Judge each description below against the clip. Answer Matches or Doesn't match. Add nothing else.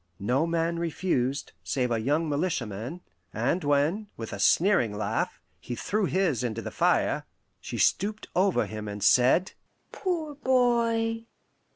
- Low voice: Doesn't match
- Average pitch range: Doesn't match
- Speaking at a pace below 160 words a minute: Matches